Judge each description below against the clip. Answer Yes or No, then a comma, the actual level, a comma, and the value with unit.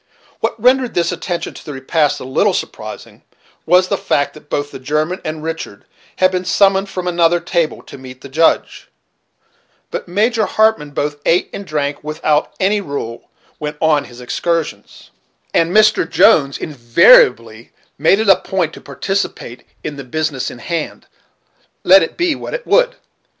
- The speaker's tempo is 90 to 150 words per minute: No, average, 165 wpm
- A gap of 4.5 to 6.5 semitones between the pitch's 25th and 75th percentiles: Yes, average, 4.9 semitones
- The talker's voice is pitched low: No, medium, 165 Hz